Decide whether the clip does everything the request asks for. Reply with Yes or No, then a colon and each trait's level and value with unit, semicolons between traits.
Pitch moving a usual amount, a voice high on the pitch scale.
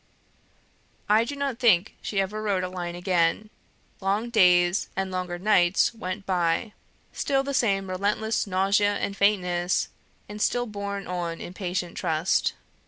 Yes: average, 3.0 semitones; high, 195 Hz